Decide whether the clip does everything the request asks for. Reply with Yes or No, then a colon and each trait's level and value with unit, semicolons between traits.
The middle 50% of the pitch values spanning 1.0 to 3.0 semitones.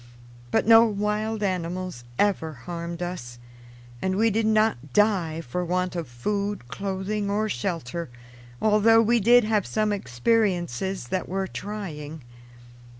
No: average, 4.0 semitones